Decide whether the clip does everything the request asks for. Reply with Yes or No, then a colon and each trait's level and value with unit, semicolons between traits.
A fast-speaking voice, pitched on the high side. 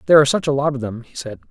No: fast, 360 wpm; low, 135 Hz